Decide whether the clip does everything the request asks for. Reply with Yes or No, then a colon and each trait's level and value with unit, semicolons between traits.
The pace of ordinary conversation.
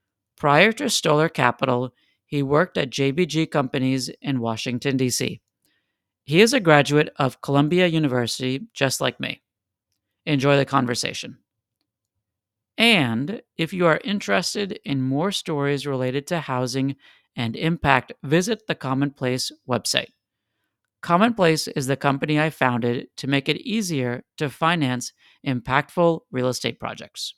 No: slow, 125 wpm